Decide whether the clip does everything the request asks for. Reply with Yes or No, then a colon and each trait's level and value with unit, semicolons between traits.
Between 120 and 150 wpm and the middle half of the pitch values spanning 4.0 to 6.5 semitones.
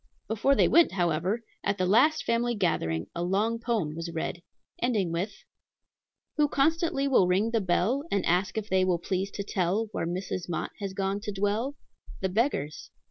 No: average, 180 wpm; average, 4.5 semitones